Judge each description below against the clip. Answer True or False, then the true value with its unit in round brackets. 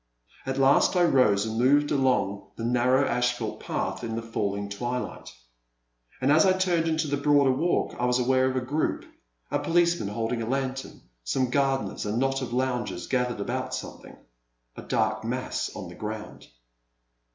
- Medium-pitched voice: False (130 Hz)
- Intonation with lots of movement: False (3.2 semitones)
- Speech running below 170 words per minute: False (175 wpm)